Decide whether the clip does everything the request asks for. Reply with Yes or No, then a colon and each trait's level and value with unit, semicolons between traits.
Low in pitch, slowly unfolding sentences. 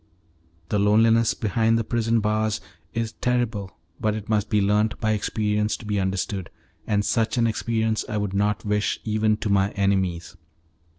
No: low, 105 Hz; average, 165 wpm